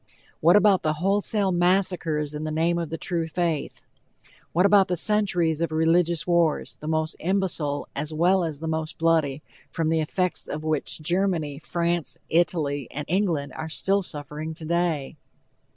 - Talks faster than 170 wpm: No, average, 160 wpm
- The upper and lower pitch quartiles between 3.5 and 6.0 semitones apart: No, narrow, 2.5 semitones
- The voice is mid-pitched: Yes, medium, 165 Hz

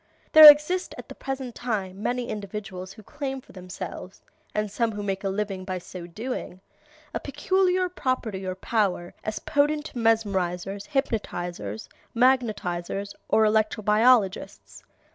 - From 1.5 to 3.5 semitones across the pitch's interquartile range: No, average, 5.2 semitones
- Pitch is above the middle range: Yes, high, 215 Hz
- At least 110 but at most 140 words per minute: Yes, slow, 135 wpm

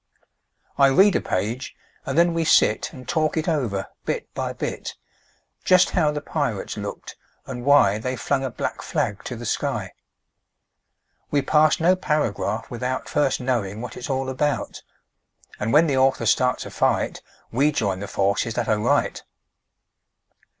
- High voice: No, low, 130 Hz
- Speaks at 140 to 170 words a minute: Yes, average, 160 wpm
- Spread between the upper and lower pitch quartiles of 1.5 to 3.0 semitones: No, average, 4.8 semitones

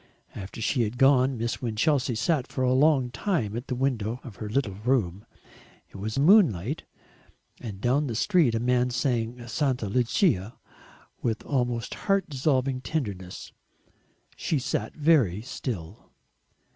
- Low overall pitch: Yes, low, 125 Hz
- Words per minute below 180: Yes, average, 140 wpm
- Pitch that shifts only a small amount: No, average, 3.8 semitones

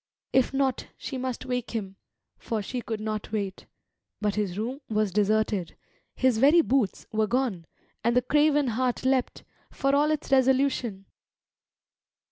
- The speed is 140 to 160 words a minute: Yes, average, 145 wpm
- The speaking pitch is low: No, high, 240 Hz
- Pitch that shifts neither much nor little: Yes, average, 3.9 semitones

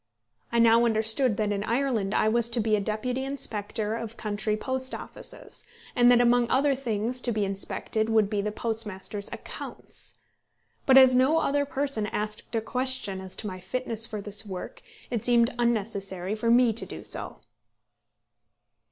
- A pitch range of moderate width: Yes, average, 3.0 semitones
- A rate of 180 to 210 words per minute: No, average, 170 wpm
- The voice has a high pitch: Yes, high, 225 Hz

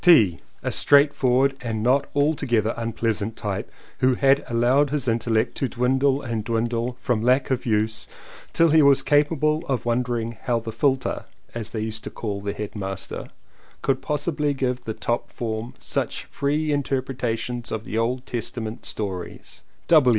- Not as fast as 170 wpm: Yes, average, 160 wpm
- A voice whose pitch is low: Yes, low, 120 Hz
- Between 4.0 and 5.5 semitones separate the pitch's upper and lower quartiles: No, average, 3.5 semitones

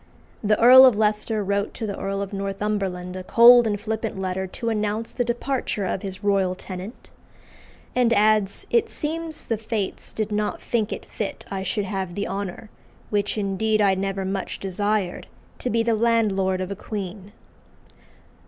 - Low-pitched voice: No, high, 205 Hz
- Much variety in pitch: No, narrow, 2.4 semitones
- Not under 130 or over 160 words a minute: No, average, 170 wpm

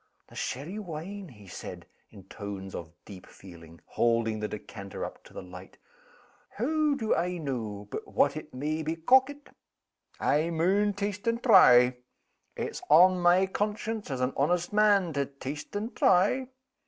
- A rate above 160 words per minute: No, average, 155 wpm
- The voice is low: No, medium, 160 Hz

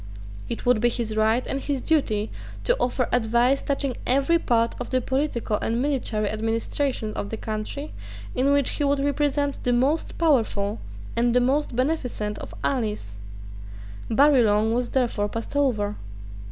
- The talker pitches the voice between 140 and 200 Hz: No, high, 245 Hz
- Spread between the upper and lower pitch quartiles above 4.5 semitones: No, average, 4.0 semitones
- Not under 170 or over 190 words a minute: No, average, 155 wpm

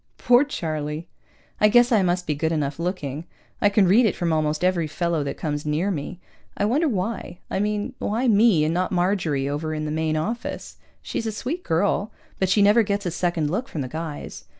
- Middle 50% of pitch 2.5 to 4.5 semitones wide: No, average, 5.0 semitones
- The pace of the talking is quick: Yes, fast, 210 wpm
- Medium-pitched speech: Yes, medium, 180 Hz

